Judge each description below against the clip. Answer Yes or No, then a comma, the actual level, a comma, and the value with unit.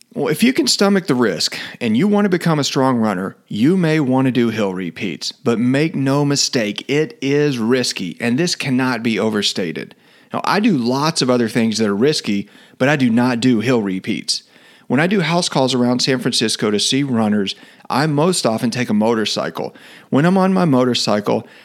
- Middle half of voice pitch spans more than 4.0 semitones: Yes, wide, 5.5 semitones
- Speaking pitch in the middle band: No, low, 130 Hz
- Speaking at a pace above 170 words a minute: Yes, average, 200 wpm